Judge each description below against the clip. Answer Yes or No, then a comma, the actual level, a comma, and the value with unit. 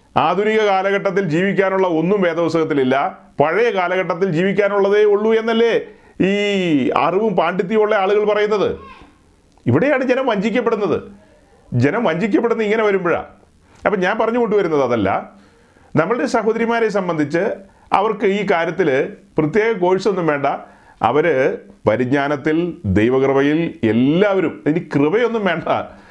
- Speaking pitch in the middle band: No, high, 200 Hz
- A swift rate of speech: No, average, 100 wpm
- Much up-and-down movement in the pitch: No, average, 4.9 semitones